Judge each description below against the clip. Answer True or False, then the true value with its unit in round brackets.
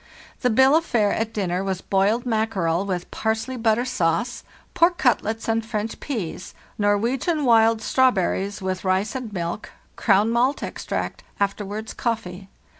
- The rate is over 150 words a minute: False (145 wpm)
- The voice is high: True (220 Hz)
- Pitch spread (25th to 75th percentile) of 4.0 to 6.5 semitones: False (3.6 semitones)